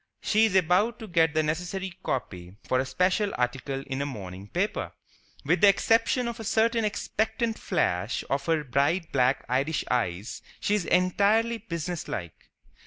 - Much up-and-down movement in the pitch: Yes, wide, 8.0 semitones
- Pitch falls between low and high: Yes, medium, 170 Hz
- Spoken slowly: No, average, 160 wpm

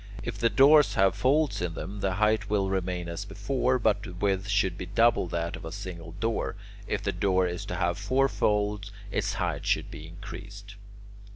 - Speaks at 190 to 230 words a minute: Yes, average, 195 wpm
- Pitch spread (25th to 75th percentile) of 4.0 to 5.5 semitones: No, narrow, 2.6 semitones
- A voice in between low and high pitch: No, low, 100 Hz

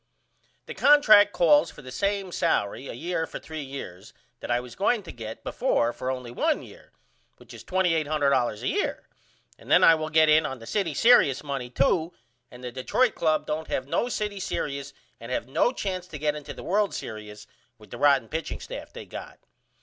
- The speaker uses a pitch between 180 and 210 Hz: No, medium, 150 Hz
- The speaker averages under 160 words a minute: No, average, 200 wpm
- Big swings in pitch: Yes, wide, 6.2 semitones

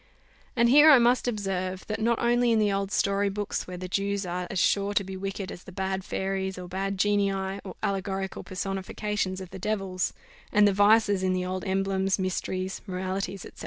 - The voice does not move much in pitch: Yes, narrow, 1.5 semitones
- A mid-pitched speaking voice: No, high, 195 Hz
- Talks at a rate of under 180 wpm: No, average, 200 wpm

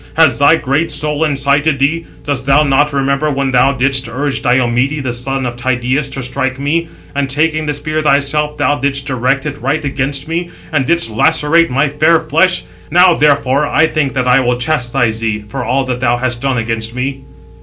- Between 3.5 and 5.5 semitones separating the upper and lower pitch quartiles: No, average, 2.8 semitones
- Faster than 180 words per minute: Yes, average, 195 wpm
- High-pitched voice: No, medium, 140 Hz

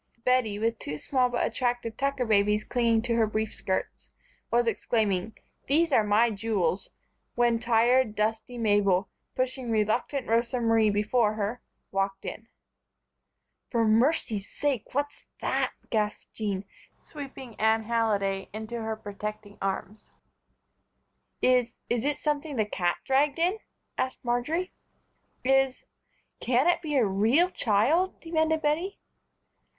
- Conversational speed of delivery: No, slow, 130 wpm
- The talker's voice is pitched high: Yes, high, 230 Hz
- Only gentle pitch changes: No, average, 3.6 semitones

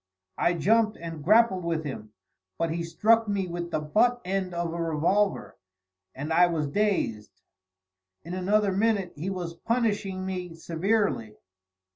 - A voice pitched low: No, medium, 180 Hz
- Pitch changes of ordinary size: Yes, average, 3.8 semitones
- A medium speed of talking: Yes, average, 145 wpm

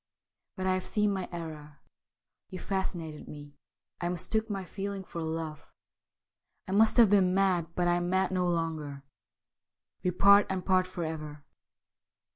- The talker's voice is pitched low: No, medium, 180 Hz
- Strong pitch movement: No, average, 3.0 semitones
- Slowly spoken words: No, average, 160 wpm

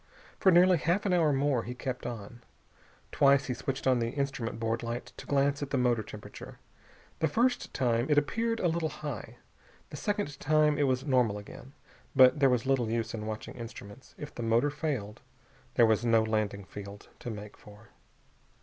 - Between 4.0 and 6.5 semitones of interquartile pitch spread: Yes, average, 4.4 semitones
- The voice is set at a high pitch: No, low, 130 Hz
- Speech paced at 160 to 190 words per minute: Yes, average, 185 wpm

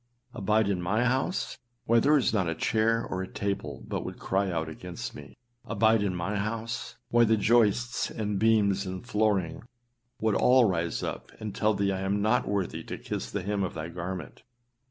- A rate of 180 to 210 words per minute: Yes, average, 195 wpm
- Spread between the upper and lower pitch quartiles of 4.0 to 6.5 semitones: No, average, 3.2 semitones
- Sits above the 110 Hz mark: No, low, 105 Hz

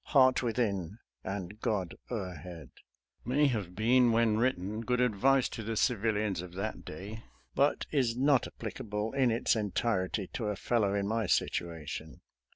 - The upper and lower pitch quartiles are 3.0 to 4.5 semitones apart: Yes, average, 4.1 semitones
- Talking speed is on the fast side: No, average, 155 wpm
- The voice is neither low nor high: No, low, 110 Hz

